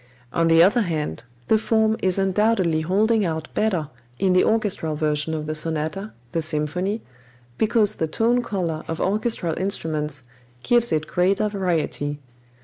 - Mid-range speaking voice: Yes, medium, 180 Hz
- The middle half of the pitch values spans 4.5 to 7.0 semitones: Yes, average, 5.3 semitones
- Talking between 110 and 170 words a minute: Yes, average, 145 wpm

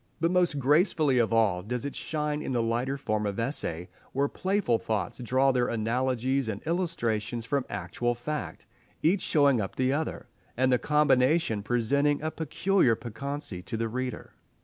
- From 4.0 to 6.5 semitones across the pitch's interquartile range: Yes, average, 4.4 semitones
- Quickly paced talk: No, average, 165 wpm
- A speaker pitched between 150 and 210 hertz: No, low, 130 Hz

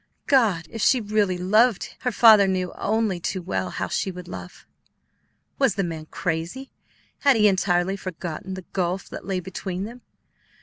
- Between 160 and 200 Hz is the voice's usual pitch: Yes, high, 190 Hz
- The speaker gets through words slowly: No, average, 165 wpm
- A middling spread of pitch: Yes, average, 3.3 semitones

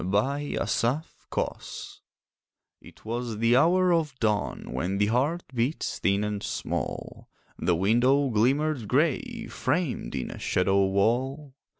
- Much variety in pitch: Yes, wide, 5.9 semitones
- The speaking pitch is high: No, low, 125 Hz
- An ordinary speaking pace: No, slow, 120 wpm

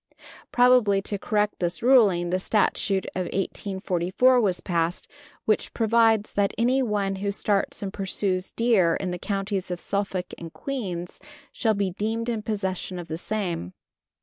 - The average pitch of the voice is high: Yes, high, 200 Hz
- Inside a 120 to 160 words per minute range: Yes, average, 150 wpm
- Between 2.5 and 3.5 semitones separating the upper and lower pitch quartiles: Yes, average, 3.1 semitones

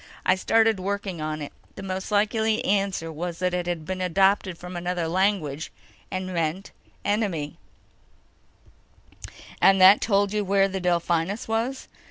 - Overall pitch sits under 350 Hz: Yes, medium, 185 Hz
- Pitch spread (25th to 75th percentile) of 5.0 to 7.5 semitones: No, narrow, 2.6 semitones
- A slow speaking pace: No, average, 145 wpm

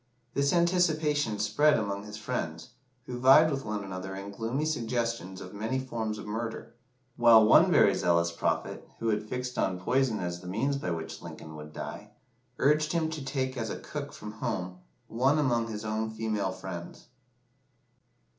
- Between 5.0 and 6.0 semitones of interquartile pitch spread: Yes, wide, 5.4 semitones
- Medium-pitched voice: No, low, 110 Hz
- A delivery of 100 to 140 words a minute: No, average, 170 wpm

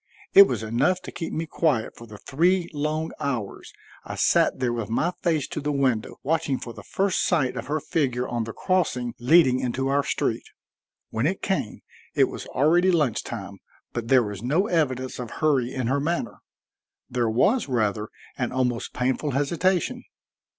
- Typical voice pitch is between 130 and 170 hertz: Yes, low, 135 Hz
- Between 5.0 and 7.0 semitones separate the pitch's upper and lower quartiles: Yes, average, 5.3 semitones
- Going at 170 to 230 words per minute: Yes, average, 180 wpm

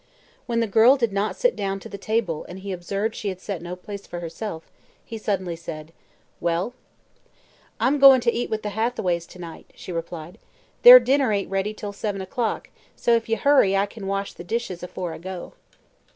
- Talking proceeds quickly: Yes, fast, 210 wpm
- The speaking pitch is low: No, high, 200 Hz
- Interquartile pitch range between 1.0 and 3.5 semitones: No, average, 4.1 semitones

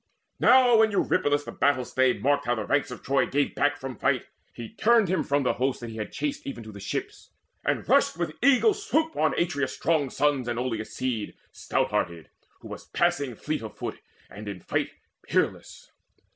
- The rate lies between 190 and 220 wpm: Yes, average, 200 wpm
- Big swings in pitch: No, average, 4.8 semitones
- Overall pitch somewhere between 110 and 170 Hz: Yes, medium, 140 Hz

